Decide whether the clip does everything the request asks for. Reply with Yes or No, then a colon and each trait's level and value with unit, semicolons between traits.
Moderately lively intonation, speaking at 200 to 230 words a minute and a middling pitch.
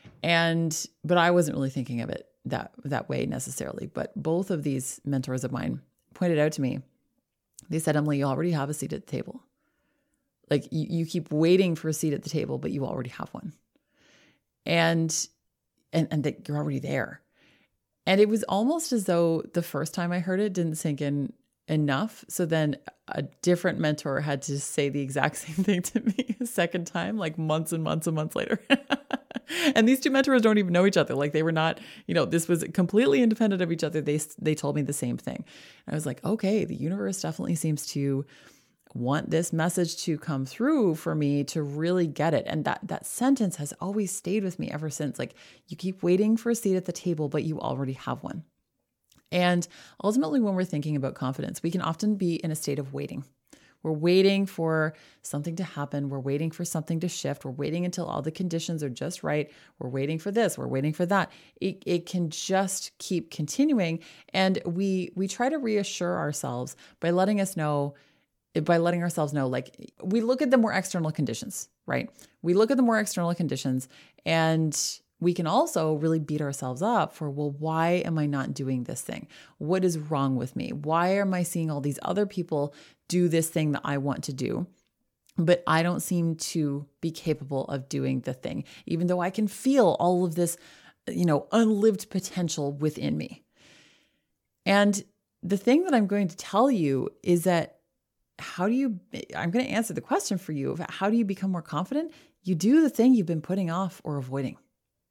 Yes: average, 4.5 semitones; fast, 205 wpm; medium, 170 Hz